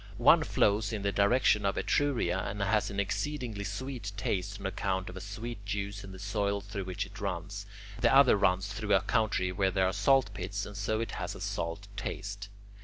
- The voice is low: Yes, low, 100 Hz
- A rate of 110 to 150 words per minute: No, fast, 205 wpm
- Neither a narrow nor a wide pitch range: No, narrow, 1.6 semitones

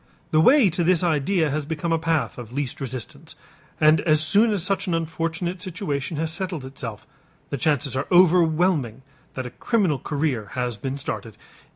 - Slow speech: No, average, 175 wpm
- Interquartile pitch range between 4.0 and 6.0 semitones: Yes, average, 4.4 semitones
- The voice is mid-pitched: Yes, medium, 155 Hz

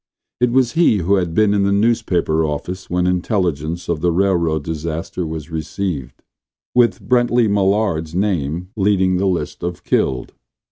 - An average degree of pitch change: Yes, average, 3.9 semitones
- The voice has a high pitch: No, very low, 90 Hz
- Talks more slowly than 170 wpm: Yes, average, 150 wpm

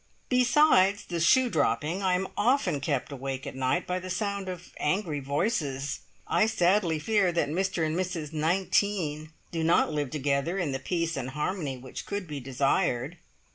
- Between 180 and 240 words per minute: No, average, 170 wpm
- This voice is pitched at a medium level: Yes, medium, 170 Hz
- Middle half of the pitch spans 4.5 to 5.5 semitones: Yes, average, 4.9 semitones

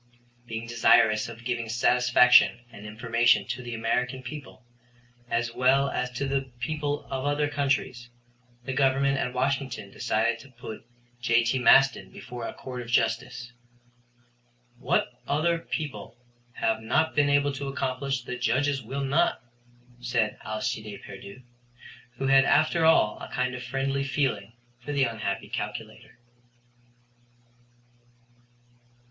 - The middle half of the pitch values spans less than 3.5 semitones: Yes, average, 2.7 semitones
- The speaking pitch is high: No, low, 125 Hz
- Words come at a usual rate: No, slow, 130 wpm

